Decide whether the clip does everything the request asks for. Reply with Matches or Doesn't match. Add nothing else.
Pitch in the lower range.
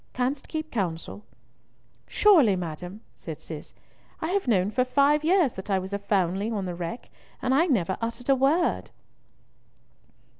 Doesn't match